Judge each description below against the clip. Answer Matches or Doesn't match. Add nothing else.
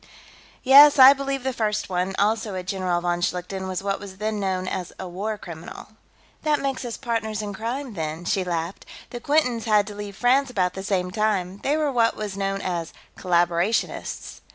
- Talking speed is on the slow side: Doesn't match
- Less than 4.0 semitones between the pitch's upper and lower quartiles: Doesn't match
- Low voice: Doesn't match